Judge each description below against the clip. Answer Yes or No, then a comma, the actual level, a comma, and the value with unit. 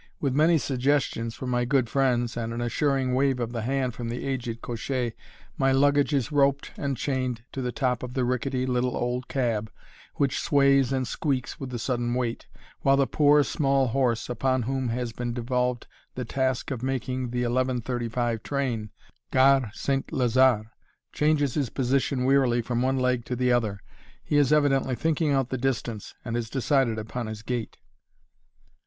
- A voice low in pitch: Yes, low, 125 Hz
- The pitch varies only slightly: Yes, narrow, 2.2 semitones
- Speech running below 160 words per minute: No, average, 175 wpm